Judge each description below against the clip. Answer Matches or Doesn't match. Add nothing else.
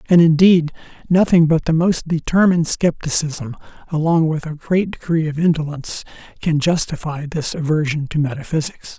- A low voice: Doesn't match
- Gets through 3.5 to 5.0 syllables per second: Doesn't match